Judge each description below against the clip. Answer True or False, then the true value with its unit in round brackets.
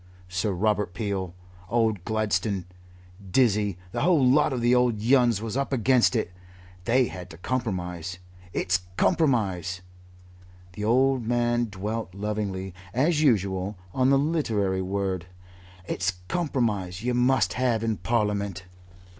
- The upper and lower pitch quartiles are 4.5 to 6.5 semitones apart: True (4.8 semitones)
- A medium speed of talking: False (130 wpm)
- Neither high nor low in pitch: False (110 Hz)